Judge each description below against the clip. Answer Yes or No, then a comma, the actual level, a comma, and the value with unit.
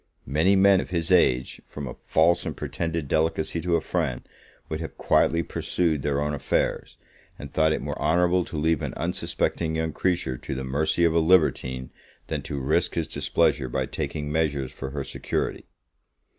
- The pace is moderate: Yes, average, 180 wpm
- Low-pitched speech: Yes, very low, 80 Hz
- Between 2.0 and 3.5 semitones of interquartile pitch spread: Yes, average, 3.0 semitones